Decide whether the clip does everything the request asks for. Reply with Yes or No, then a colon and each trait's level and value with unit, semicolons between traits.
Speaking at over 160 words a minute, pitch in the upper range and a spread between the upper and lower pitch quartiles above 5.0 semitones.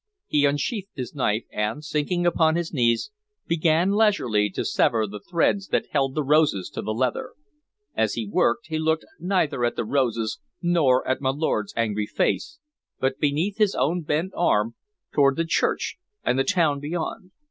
No: average, 170 wpm; medium, 150 Hz; wide, 5.5 semitones